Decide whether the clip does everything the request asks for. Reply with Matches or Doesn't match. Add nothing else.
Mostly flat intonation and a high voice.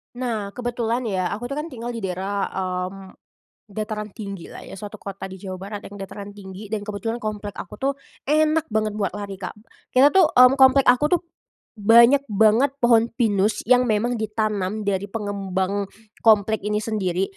Doesn't match